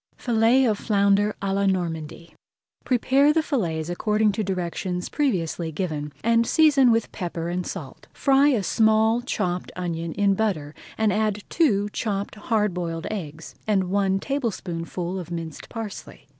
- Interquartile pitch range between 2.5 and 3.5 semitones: No, average, 4.4 semitones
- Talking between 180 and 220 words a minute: No, average, 145 wpm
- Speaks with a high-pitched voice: Yes, high, 200 Hz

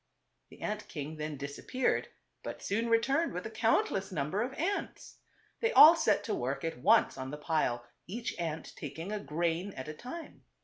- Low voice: No, medium, 180 Hz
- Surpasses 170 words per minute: Yes, average, 190 wpm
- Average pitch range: No, wide, 7.3 semitones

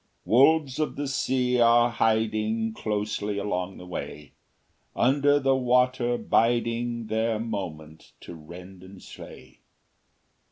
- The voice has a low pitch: Yes, low, 115 Hz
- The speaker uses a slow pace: Yes, slow, 115 wpm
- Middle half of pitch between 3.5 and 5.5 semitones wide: Yes, average, 3.8 semitones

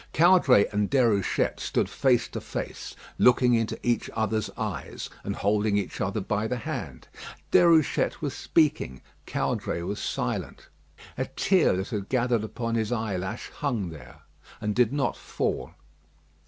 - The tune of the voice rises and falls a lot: No, average, 3.6 semitones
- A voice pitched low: Yes, low, 115 Hz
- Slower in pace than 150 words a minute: Yes, average, 140 wpm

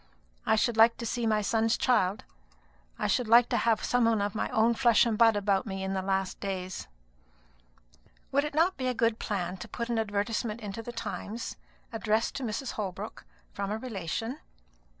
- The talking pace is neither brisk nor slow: Yes, average, 190 wpm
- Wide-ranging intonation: No, average, 2.7 semitones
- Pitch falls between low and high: No, high, 225 Hz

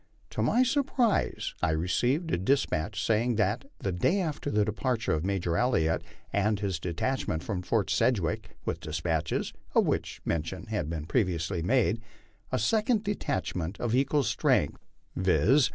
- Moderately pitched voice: No, low, 105 Hz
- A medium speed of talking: Yes, average, 150 wpm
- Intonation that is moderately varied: No, wide, 7.1 semitones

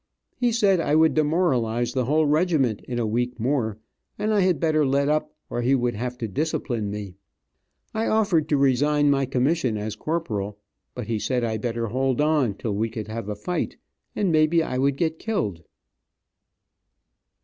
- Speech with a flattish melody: No, wide, 5.5 semitones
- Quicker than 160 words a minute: Yes, average, 180 wpm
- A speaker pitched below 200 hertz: Yes, low, 135 Hz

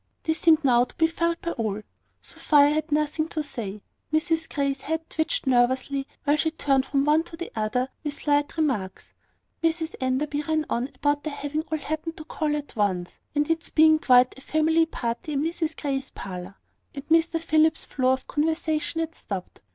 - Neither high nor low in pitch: No, very high, 300 Hz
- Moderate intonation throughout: Yes, average, 3.4 semitones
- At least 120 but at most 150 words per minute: No, average, 180 wpm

